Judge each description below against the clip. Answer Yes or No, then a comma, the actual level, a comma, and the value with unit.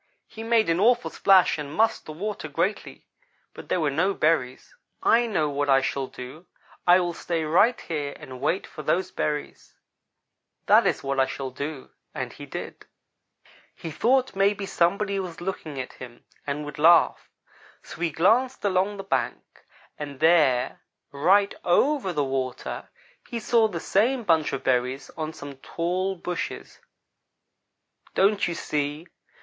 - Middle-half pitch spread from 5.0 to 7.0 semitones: Yes, wide, 5.5 semitones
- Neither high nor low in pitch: Yes, medium, 170 Hz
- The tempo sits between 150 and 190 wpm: Yes, average, 155 wpm